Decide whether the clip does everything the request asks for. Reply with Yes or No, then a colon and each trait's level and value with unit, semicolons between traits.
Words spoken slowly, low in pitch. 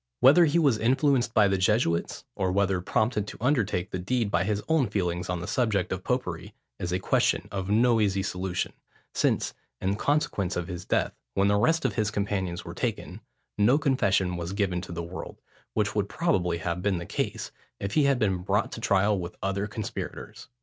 No: average, 200 wpm; low, 100 Hz